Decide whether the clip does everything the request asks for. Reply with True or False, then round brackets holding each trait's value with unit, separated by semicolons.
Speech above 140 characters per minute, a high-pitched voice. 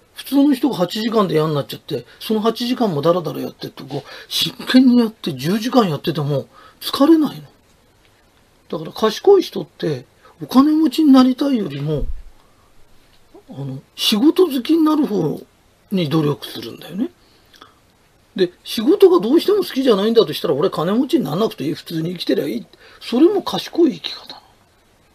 True (330 characters per minute; 225 Hz)